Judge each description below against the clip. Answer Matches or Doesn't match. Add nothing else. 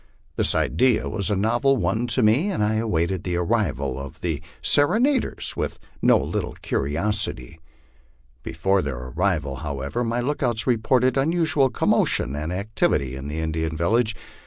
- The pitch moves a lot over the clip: Matches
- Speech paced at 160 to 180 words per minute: Doesn't match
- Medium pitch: Doesn't match